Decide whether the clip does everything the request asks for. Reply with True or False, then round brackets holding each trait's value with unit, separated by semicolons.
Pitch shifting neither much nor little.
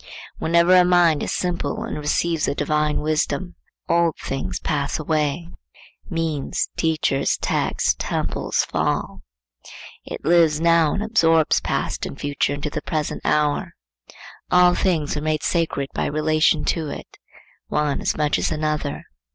False (2.3 semitones)